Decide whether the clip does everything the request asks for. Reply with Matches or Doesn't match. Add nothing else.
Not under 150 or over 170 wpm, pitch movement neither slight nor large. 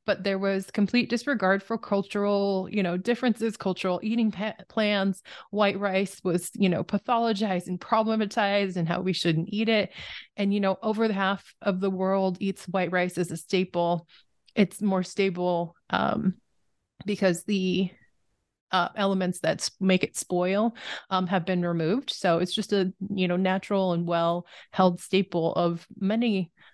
Doesn't match